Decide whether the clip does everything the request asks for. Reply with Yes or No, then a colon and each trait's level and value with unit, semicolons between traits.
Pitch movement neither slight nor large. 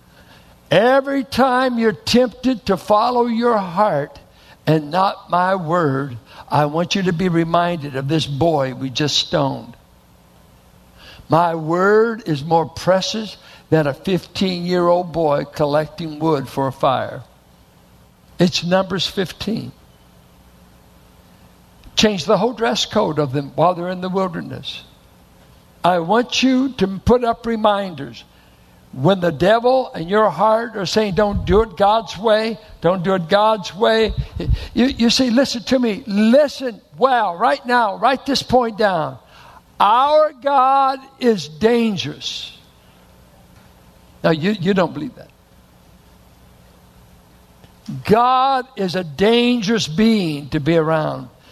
No: wide, 8.0 semitones